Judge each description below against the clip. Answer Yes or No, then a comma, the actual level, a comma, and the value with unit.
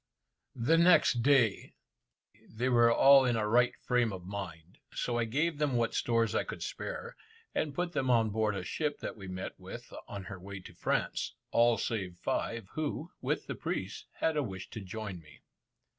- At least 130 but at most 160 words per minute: No, average, 190 wpm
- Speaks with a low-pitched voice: Yes, low, 115 Hz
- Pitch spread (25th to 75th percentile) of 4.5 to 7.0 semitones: Yes, average, 5.2 semitones